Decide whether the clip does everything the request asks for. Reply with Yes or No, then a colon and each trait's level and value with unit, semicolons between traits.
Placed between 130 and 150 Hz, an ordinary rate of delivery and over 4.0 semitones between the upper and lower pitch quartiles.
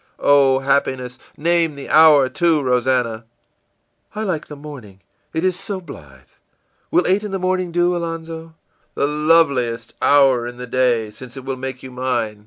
Yes: medium, 140 Hz; average, 170 wpm; average, 4.7 semitones